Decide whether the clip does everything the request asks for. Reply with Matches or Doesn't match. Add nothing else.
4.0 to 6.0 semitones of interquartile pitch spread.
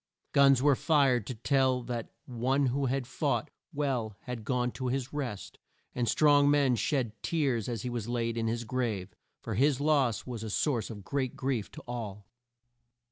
Doesn't match